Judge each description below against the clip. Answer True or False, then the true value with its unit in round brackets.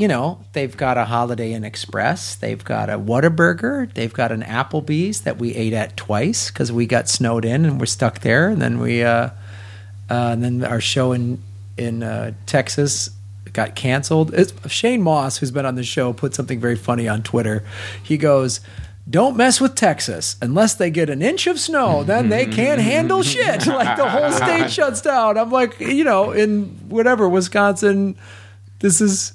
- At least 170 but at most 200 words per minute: True (190 wpm)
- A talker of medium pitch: False (120 Hz)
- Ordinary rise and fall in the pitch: False (7.8 semitones)